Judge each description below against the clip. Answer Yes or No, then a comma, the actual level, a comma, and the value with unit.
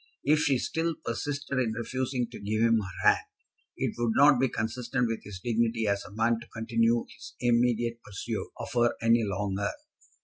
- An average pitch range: No, narrow, 2.0 semitones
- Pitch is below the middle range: Yes, low, 115 Hz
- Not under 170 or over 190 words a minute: Yes, average, 180 wpm